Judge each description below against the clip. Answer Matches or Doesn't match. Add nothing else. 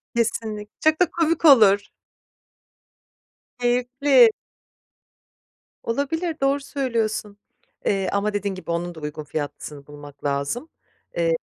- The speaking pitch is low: Doesn't match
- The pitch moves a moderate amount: Doesn't match